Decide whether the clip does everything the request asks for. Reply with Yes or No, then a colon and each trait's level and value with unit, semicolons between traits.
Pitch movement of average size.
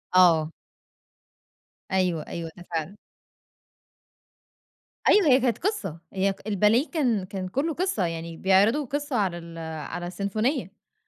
No: wide, 6.9 semitones